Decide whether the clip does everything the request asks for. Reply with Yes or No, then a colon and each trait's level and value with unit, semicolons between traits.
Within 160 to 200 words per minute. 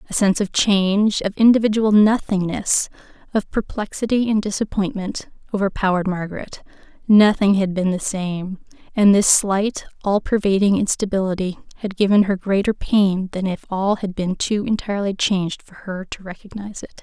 No: average, 150 wpm